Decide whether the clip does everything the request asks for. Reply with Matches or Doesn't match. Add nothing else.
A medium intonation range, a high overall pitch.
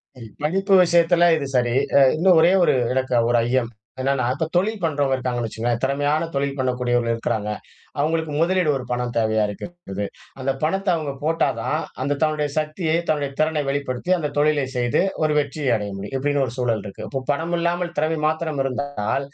Doesn't match